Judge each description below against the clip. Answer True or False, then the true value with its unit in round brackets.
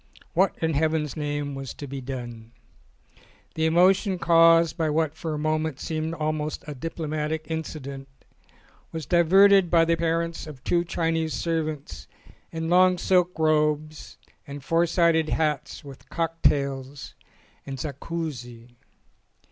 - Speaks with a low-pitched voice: False (160 Hz)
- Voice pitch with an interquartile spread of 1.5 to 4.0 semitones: True (2.4 semitones)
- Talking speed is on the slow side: True (130 wpm)